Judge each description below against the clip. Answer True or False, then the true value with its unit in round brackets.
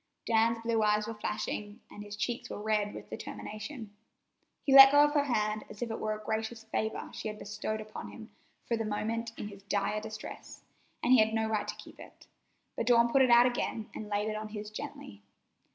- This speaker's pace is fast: True (220 wpm)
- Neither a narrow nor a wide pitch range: False (1.7 semitones)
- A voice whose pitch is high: True (220 Hz)